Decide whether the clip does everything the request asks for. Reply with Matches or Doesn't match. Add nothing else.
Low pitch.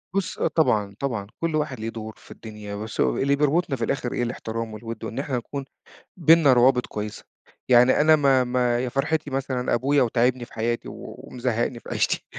Matches